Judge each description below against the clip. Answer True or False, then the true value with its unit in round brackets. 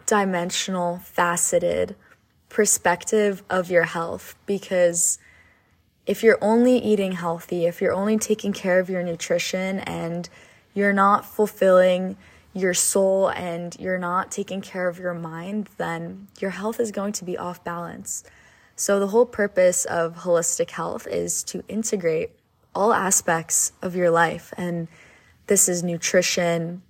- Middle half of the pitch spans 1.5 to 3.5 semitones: True (2.7 semitones)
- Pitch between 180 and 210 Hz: True (185 Hz)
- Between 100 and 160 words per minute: True (140 wpm)